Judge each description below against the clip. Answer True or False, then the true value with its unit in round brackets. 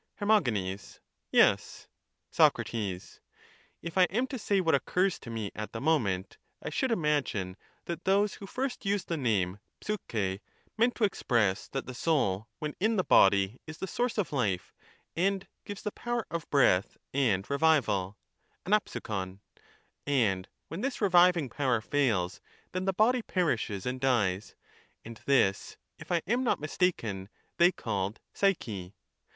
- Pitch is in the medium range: True (145 Hz)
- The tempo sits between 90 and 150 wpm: True (145 wpm)